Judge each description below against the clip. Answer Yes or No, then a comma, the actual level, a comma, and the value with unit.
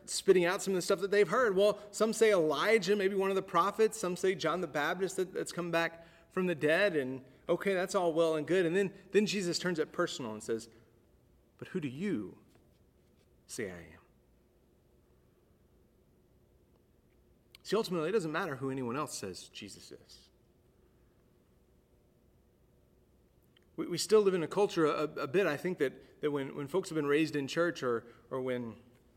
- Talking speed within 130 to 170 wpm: No, average, 180 wpm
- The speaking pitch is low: No, medium, 170 Hz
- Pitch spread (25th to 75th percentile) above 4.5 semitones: Yes, average, 5.2 semitones